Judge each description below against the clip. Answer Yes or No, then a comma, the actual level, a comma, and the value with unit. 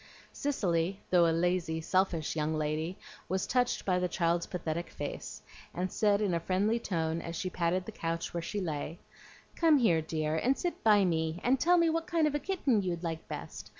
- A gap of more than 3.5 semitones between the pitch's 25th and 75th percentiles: Yes, average, 4.7 semitones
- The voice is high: No, medium, 180 Hz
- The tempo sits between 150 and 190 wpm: No, average, 200 wpm